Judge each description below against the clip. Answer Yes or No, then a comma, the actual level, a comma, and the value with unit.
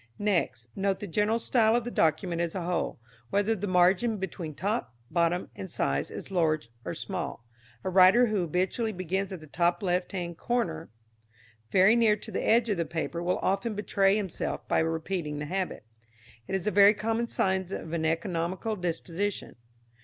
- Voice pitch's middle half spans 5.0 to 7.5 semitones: No, average, 3.5 semitones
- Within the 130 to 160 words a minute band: No, average, 180 wpm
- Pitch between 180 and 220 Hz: Yes, medium, 185 Hz